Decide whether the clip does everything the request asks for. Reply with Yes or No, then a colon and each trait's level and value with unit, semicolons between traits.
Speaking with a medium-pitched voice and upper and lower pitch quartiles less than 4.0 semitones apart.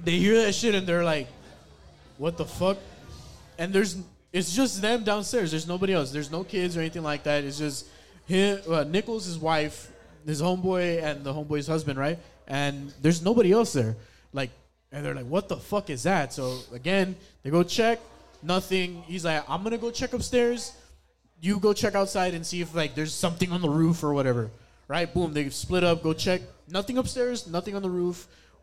No: medium, 175 Hz; average, 4.6 semitones